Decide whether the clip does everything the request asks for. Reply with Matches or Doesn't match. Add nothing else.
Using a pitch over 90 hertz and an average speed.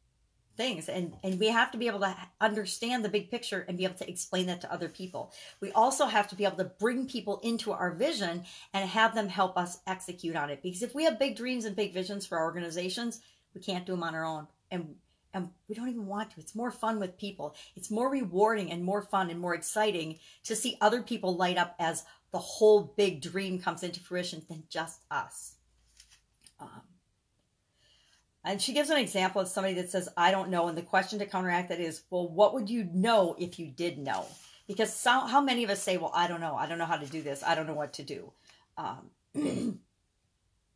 Doesn't match